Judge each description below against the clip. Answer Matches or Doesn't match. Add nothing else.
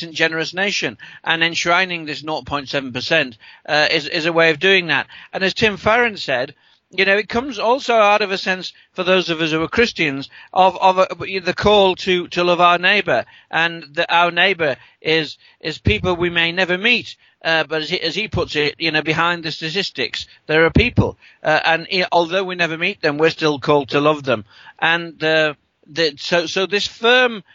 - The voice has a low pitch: Doesn't match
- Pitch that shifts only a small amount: Doesn't match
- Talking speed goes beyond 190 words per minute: Matches